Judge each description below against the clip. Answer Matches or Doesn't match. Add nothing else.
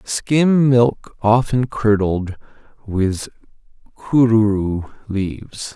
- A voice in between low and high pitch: Doesn't match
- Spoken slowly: Matches